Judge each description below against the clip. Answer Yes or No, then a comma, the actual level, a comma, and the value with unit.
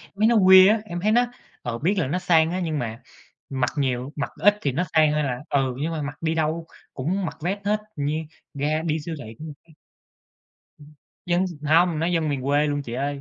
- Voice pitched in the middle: Yes, medium, 155 Hz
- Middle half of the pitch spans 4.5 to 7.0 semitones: No, average, 3.8 semitones